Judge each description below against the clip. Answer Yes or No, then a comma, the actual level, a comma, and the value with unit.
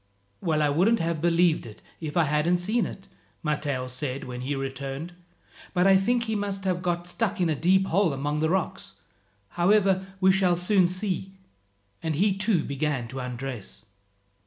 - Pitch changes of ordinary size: Yes, average, 4.9 semitones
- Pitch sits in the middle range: Yes, medium, 170 Hz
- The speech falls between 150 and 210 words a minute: Yes, average, 170 wpm